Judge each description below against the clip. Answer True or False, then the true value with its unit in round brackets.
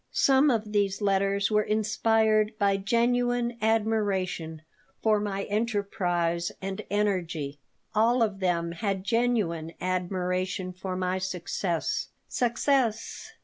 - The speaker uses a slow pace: True (105 wpm)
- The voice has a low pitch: False (200 Hz)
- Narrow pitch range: False (3.3 semitones)